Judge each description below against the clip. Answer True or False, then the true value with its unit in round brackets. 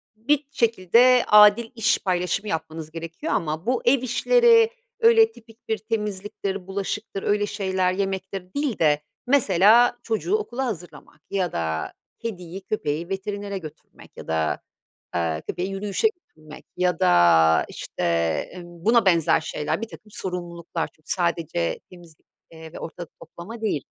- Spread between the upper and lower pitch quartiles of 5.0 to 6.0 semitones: True (5.4 semitones)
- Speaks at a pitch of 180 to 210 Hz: True (190 Hz)